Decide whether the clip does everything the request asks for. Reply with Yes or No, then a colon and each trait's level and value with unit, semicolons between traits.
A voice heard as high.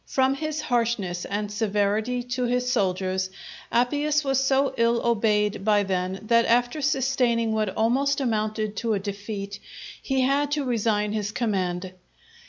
Yes: high, 230 Hz